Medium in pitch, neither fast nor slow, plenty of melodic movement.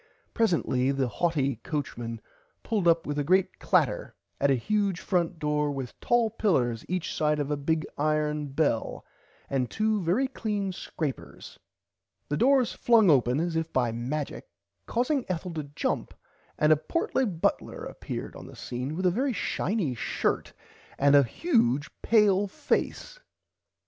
Yes: medium, 160 Hz; average, 155 wpm; wide, 6.6 semitones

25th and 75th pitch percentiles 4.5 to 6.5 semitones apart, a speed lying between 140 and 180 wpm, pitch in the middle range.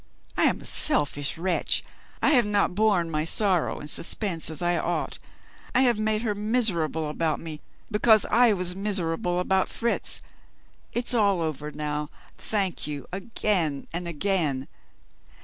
Yes: average, 5.1 semitones; average, 150 wpm; medium, 180 Hz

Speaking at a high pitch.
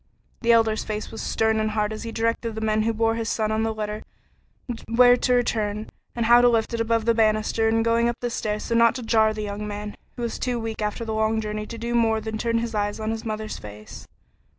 Yes: high, 220 Hz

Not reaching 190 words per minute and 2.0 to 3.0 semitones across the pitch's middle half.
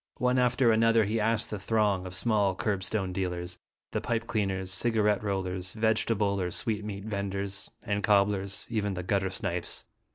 Yes: average, 155 wpm; narrow, 2.4 semitones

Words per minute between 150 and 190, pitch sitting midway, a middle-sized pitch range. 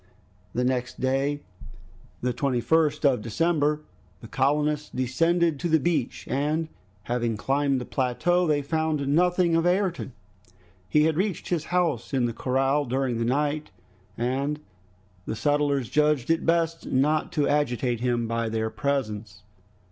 No: average, 140 wpm; medium, 145 Hz; average, 4.1 semitones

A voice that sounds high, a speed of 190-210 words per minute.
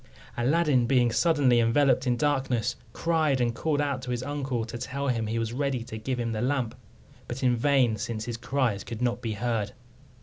No: low, 125 Hz; average, 200 wpm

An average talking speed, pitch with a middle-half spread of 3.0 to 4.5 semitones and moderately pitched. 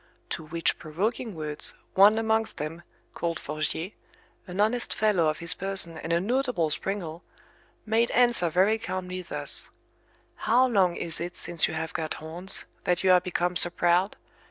Yes: average, 160 wpm; average, 4.2 semitones; medium, 180 Hz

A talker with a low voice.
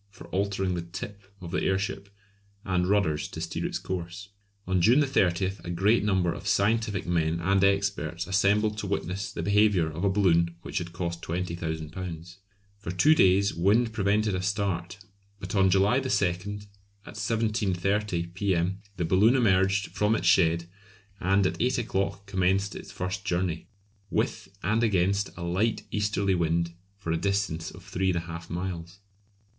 Yes: very low, 95 Hz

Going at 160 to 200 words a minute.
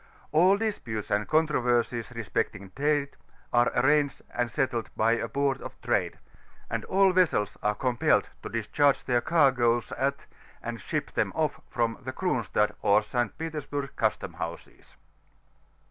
No: average, 140 wpm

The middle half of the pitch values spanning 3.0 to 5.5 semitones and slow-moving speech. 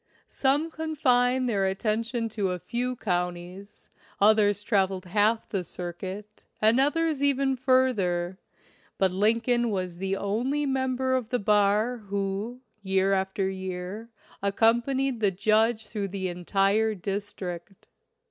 Yes: average, 4.4 semitones; slow, 125 wpm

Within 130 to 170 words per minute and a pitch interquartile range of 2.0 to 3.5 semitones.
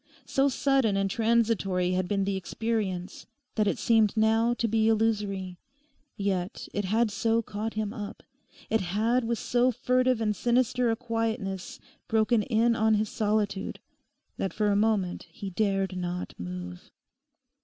Yes: average, 150 wpm; average, 2.7 semitones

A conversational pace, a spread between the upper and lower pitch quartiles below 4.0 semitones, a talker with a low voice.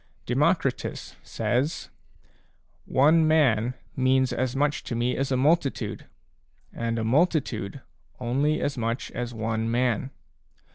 No: slow, 115 wpm; average, 3.5 semitones; low, 130 Hz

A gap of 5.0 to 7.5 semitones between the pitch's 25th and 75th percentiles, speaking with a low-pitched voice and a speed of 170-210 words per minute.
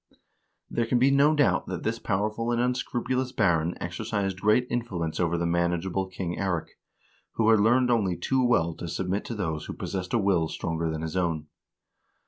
Yes: wide, 5.5 semitones; very low, 95 Hz; average, 180 wpm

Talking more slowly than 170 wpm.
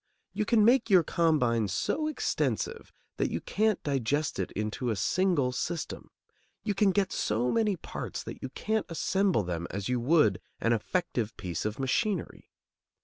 Yes: average, 160 wpm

